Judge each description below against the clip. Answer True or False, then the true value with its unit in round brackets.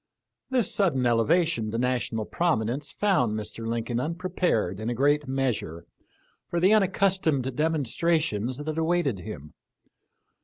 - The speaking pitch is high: False (135 Hz)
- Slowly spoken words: True (130 wpm)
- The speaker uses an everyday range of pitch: False (6.8 semitones)